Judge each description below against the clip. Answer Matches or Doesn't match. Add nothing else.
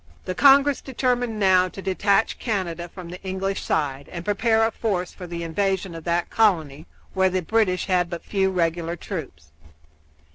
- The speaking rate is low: Doesn't match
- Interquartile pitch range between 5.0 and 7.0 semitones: Doesn't match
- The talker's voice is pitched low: Doesn't match